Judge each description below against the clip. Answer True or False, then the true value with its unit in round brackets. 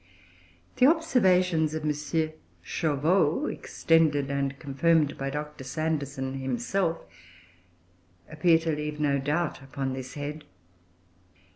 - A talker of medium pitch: True (150 Hz)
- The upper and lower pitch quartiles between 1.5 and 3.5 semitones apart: True (2.9 semitones)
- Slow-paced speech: True (105 wpm)